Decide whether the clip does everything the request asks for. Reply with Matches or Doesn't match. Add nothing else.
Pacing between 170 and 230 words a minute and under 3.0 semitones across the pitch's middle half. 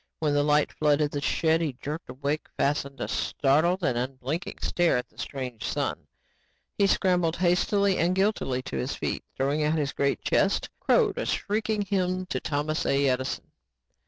Doesn't match